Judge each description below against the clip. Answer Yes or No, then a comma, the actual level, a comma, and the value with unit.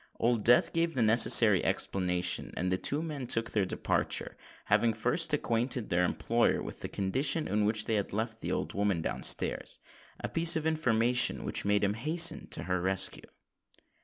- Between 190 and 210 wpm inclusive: No, average, 175 wpm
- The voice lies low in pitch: Yes, low, 115 Hz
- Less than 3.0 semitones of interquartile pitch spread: No, average, 5.0 semitones